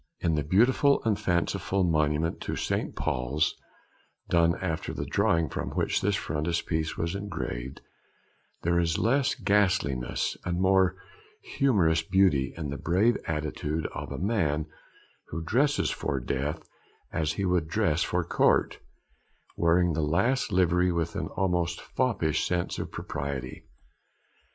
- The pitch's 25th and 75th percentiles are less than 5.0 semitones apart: Yes, average, 3.7 semitones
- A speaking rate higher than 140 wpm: No, slow, 135 wpm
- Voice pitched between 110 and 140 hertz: No, very low, 85 Hz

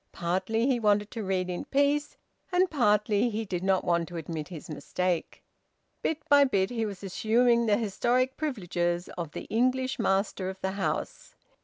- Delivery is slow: No, average, 170 wpm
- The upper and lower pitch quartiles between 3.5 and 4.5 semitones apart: No, average, 5.1 semitones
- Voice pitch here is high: Yes, high, 205 Hz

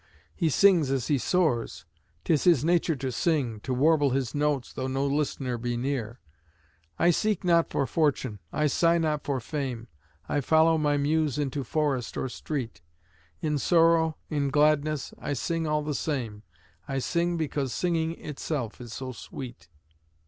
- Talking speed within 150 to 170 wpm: Yes, average, 160 wpm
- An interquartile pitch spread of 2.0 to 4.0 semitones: Yes, average, 3.6 semitones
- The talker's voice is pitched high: No, medium, 145 Hz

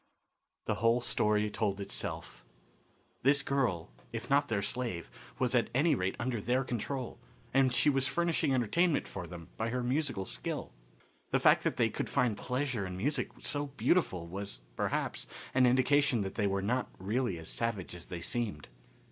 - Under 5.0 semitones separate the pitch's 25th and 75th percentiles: No, wide, 5.4 semitones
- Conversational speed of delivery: Yes, average, 170 wpm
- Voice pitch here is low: Yes, low, 120 Hz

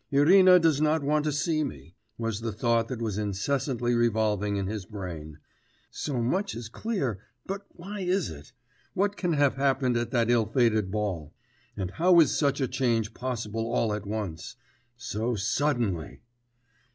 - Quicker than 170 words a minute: No, average, 165 wpm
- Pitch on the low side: Yes, low, 120 Hz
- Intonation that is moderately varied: No, wide, 5.7 semitones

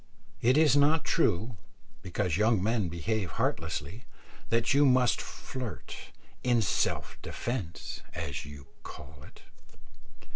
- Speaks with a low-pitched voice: Yes, low, 110 Hz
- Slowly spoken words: Yes, slow, 115 wpm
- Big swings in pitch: Yes, wide, 6.0 semitones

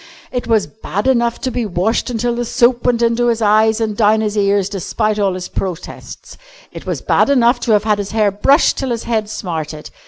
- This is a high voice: Yes, high, 220 Hz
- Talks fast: Yes, fast, 215 wpm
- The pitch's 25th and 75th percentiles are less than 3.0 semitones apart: Yes, narrow, 2.6 semitones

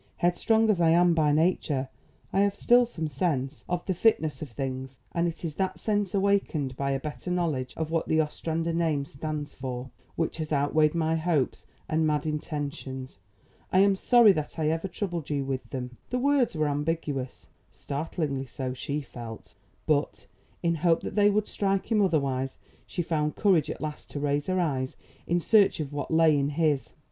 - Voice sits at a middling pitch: Yes, medium, 155 Hz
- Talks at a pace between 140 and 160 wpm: No, average, 185 wpm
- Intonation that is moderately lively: Yes, average, 3.9 semitones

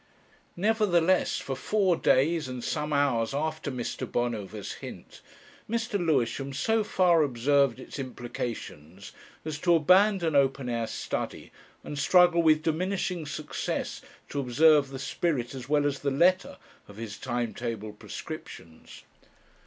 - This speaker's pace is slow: Yes, slow, 130 wpm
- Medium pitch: Yes, medium, 145 Hz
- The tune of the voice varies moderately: No, wide, 5.7 semitones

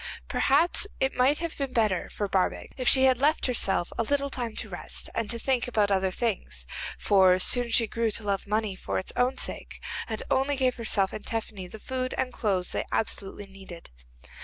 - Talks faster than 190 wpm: Yes, average, 200 wpm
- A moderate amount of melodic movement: Yes, average, 4.6 semitones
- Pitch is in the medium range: No, high, 225 Hz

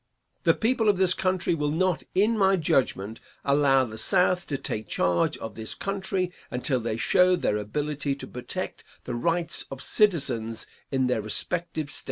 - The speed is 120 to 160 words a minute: No, average, 170 wpm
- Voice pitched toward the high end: No, medium, 150 Hz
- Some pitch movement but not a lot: No, wide, 7.2 semitones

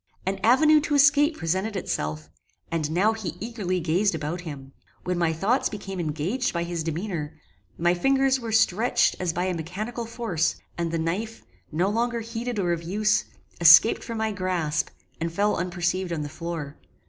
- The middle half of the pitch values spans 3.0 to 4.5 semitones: No, average, 5.1 semitones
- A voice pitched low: No, medium, 185 Hz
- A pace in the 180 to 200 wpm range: No, average, 170 wpm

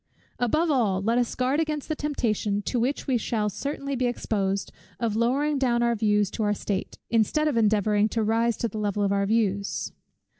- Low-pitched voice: No, high, 230 Hz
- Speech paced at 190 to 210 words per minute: Yes, average, 195 wpm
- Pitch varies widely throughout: No, average, 3.5 semitones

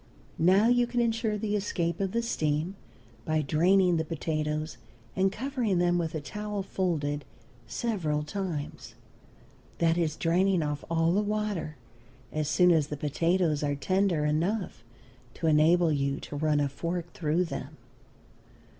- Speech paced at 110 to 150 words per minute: Yes, average, 145 wpm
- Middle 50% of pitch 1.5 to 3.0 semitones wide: No, average, 4.3 semitones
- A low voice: No, medium, 170 Hz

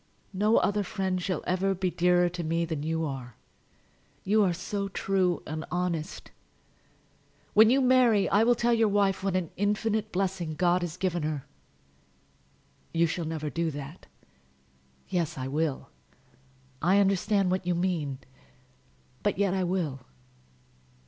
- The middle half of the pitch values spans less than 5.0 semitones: Yes, average, 3.4 semitones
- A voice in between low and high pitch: Yes, medium, 180 Hz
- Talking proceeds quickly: No, average, 145 wpm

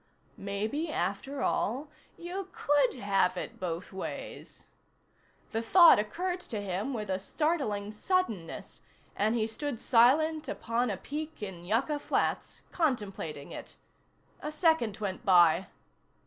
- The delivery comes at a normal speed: No, slow, 125 wpm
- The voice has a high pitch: Yes, high, 225 Hz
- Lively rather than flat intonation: Yes, wide, 7.4 semitones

